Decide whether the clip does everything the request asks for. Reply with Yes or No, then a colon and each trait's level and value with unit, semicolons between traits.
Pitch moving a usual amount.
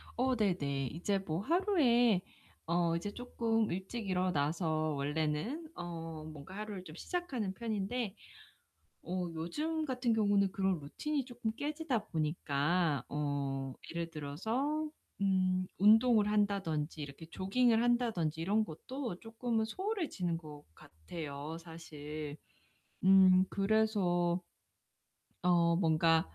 No: wide, 6.0 semitones